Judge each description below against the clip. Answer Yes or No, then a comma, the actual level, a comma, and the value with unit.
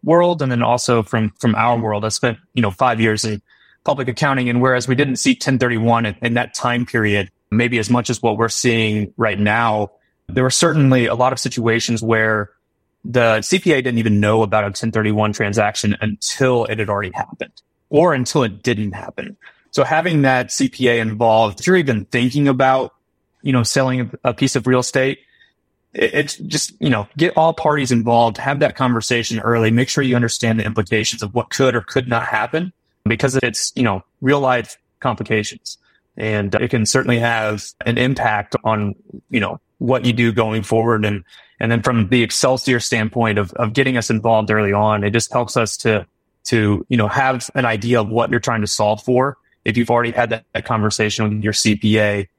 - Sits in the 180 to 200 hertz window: No, low, 115 Hz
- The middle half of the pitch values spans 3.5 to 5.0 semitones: No, average, 2.9 semitones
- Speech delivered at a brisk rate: No, average, 195 wpm